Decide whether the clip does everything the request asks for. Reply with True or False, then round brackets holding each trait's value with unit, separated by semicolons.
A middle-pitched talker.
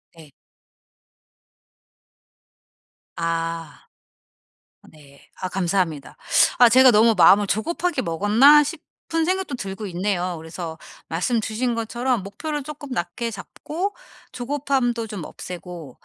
False (210 Hz)